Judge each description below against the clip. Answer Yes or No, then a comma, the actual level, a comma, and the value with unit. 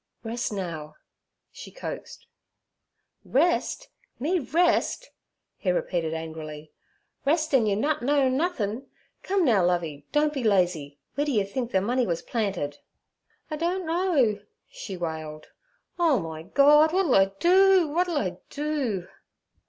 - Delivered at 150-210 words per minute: No, slow, 135 wpm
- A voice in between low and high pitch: No, high, 240 Hz